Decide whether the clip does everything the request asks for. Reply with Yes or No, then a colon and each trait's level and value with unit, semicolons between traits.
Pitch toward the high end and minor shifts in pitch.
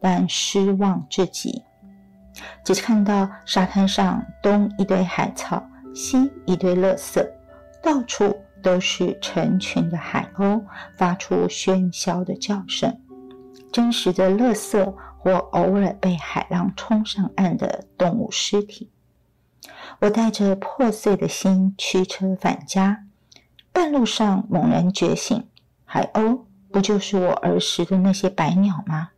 Yes: high, 195 Hz; narrow, 2.1 semitones